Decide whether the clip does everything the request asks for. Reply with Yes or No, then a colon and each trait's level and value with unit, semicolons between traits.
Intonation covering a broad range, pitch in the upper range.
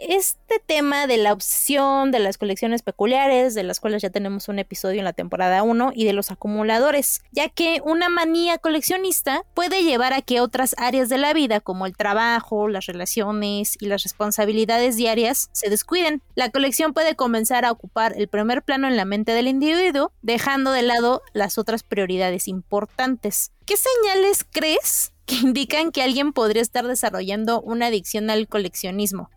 No: average, 5.0 semitones; high, 235 Hz